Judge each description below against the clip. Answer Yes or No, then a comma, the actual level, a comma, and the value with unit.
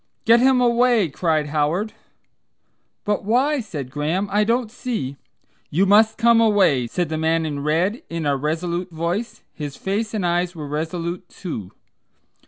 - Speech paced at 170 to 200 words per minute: No, average, 160 wpm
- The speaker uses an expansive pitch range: Yes, wide, 5.9 semitones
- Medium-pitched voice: Yes, medium, 180 Hz